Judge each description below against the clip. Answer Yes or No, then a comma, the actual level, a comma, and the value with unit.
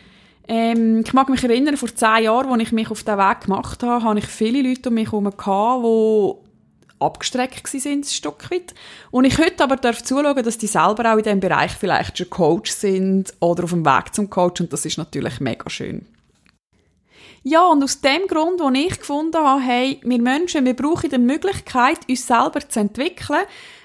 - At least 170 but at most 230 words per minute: Yes, fast, 190 wpm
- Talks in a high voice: Yes, high, 245 Hz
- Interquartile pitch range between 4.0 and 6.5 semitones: Yes, average, 4.7 semitones